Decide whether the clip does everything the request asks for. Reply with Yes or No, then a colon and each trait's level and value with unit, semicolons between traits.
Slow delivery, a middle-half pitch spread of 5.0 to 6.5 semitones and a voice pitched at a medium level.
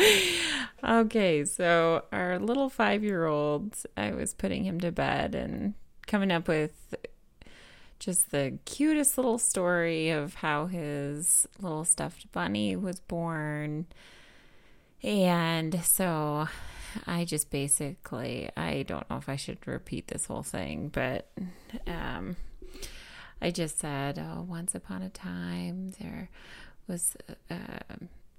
Yes: slow, 120 wpm; wide, 5.5 semitones; medium, 170 Hz